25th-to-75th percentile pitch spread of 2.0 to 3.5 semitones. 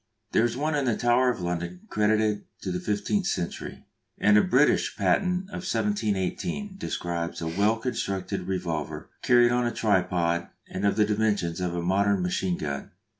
No: average, 4.9 semitones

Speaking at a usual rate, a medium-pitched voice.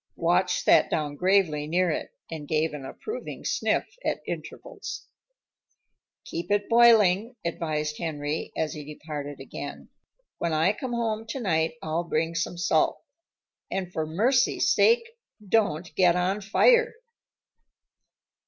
No: slow, 125 wpm; medium, 170 Hz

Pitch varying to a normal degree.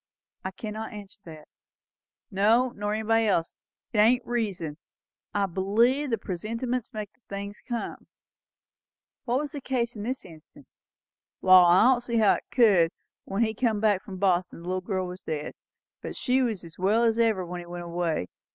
Yes: average, 4.1 semitones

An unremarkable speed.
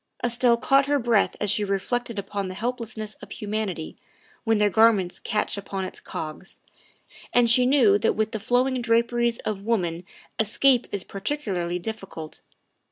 Yes: average, 160 wpm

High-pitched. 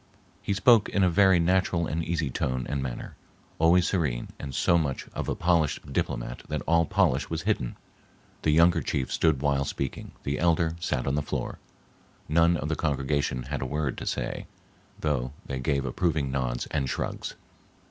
No: very low, 75 Hz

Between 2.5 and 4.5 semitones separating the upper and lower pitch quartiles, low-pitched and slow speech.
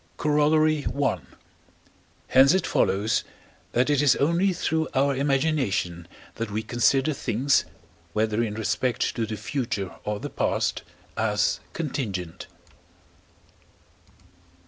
No: wide, 5.4 semitones; low, 130 Hz; slow, 110 wpm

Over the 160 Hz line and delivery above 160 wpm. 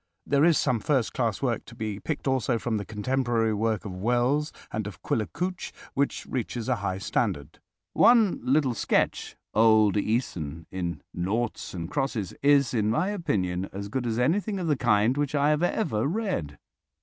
No: low, 120 Hz; average, 170 wpm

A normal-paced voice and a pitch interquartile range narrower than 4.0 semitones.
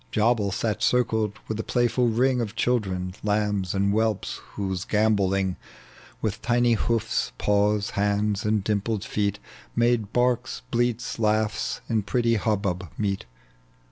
No: slow, 130 wpm; narrow, 2.5 semitones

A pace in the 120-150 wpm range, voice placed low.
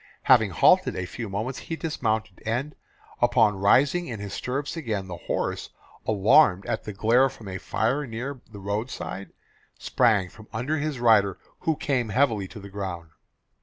No: average, 165 wpm; low, 110 Hz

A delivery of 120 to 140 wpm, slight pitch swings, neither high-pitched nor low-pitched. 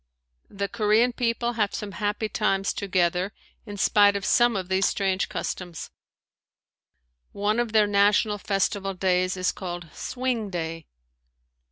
No: slow, 135 wpm; narrow, 2.3 semitones; high, 200 Hz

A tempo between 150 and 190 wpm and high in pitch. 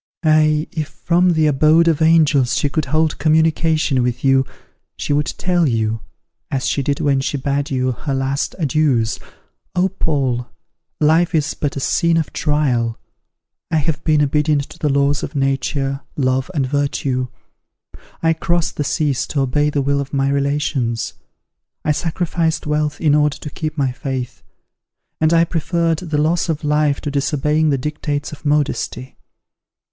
No: average, 160 wpm; medium, 150 Hz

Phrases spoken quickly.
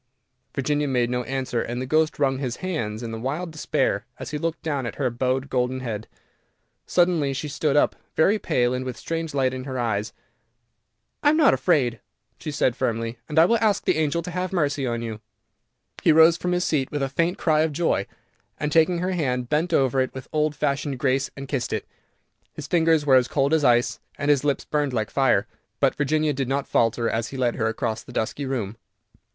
Yes: fast, 215 wpm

